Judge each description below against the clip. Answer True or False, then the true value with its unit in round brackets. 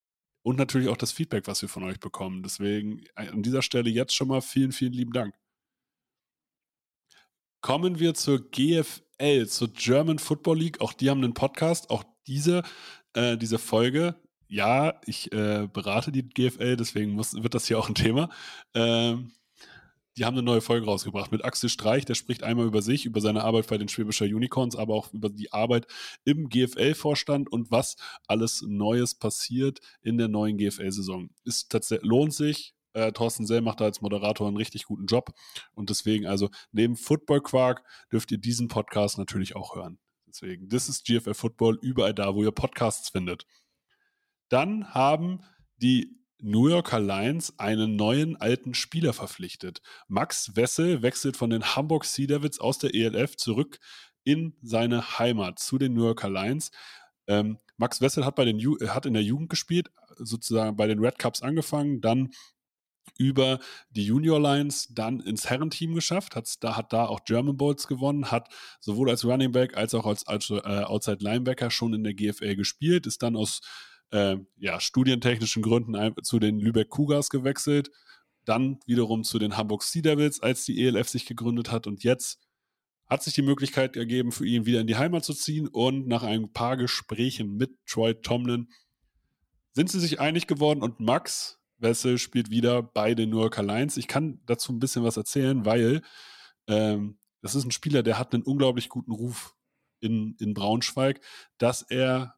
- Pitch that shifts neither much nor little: True (3.8 semitones)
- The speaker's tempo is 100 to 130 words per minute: False (175 wpm)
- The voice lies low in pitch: True (120 Hz)